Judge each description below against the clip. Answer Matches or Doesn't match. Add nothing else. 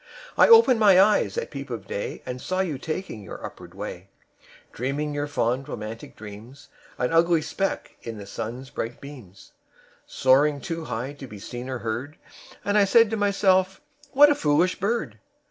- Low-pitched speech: Doesn't match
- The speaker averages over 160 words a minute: Matches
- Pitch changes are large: Matches